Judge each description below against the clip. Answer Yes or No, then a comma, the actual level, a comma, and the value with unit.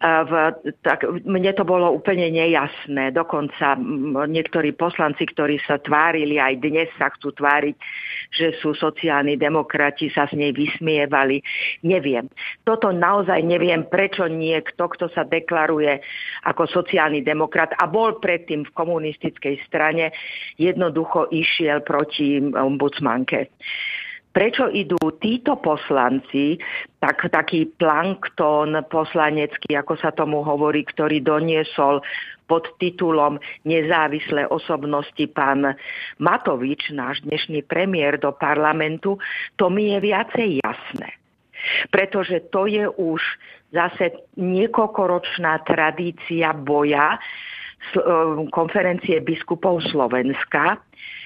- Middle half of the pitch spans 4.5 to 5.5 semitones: No, average, 2.9 semitones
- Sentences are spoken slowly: Yes, slow, 105 wpm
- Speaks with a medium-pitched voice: Yes, medium, 160 Hz